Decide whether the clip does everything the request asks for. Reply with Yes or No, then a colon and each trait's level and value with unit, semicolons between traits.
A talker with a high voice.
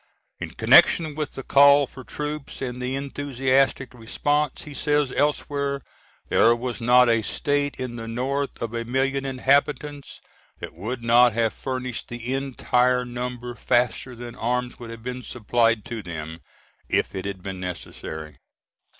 No: low, 125 Hz